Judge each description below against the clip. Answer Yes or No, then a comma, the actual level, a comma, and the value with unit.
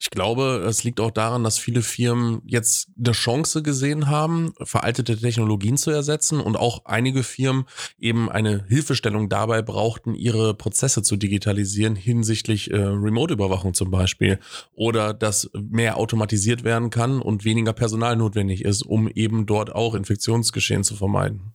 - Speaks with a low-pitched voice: Yes, low, 115 Hz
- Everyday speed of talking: Yes, average, 150 wpm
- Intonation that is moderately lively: No, narrow, 2.2 semitones